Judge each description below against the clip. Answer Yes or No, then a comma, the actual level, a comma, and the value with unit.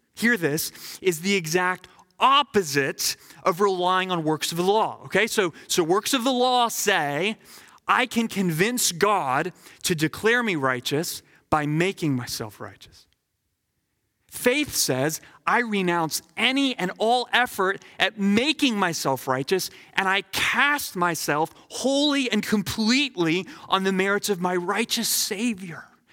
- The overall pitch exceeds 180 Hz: Yes, high, 190 Hz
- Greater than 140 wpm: No, slow, 135 wpm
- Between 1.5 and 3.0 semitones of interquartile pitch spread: No, wide, 5.6 semitones